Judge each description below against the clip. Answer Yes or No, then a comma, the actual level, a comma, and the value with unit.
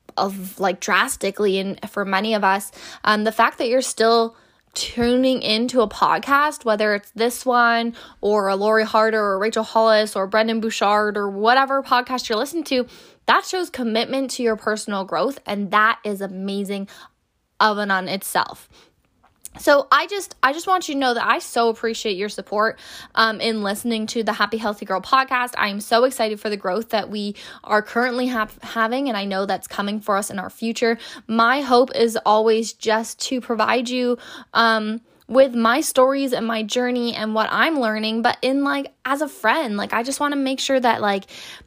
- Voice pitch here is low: No, high, 225 Hz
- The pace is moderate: Yes, average, 195 wpm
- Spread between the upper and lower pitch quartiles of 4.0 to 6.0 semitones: No, average, 3.1 semitones